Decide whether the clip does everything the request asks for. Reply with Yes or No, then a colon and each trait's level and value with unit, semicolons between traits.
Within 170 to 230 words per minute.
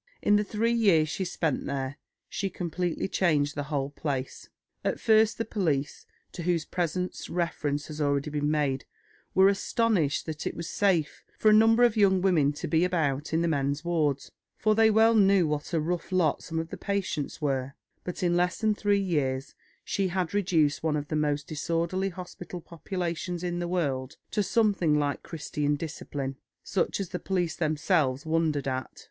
Yes: average, 180 wpm